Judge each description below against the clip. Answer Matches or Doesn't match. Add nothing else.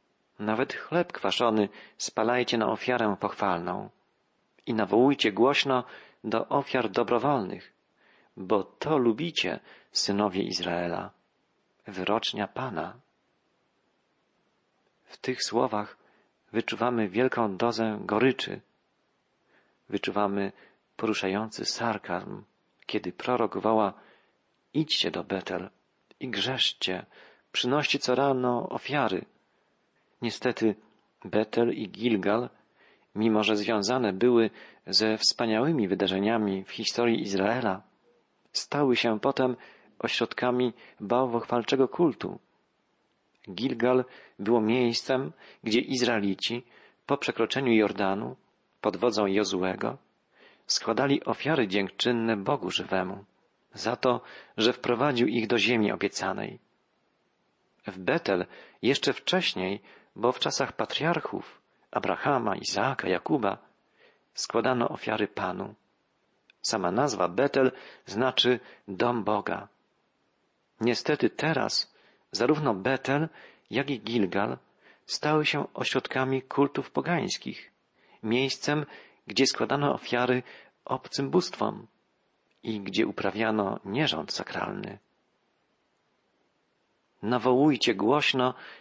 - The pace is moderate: Doesn't match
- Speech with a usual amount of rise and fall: Matches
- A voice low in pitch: Matches